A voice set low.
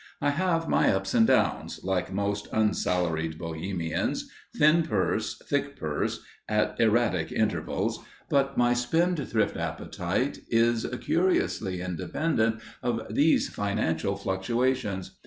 Yes: low, 110 Hz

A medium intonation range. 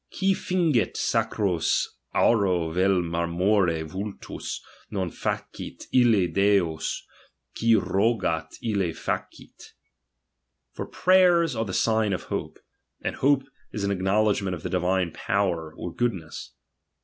Yes: average, 4.3 semitones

